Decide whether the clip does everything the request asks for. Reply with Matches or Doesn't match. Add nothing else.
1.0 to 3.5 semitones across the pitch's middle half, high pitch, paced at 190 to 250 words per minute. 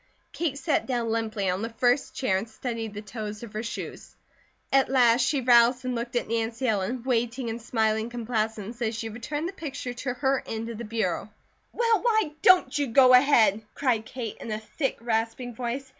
Matches